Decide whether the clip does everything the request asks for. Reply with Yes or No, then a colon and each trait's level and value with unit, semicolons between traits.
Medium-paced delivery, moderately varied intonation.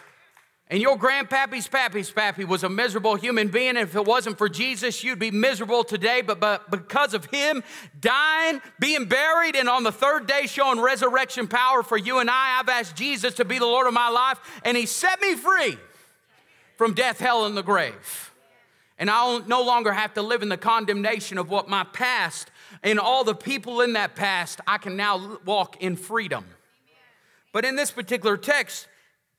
Yes: average, 190 wpm; average, 3.6 semitones